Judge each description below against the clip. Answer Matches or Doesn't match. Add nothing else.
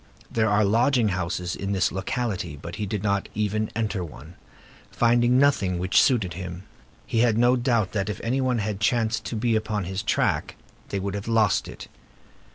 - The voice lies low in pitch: Matches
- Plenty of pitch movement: Doesn't match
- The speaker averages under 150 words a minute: Doesn't match